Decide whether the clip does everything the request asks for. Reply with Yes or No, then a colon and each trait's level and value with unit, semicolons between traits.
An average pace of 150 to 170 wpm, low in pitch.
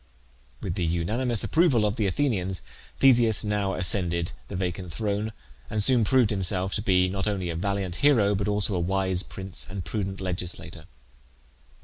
Yes: average, 160 wpm; very low, 95 Hz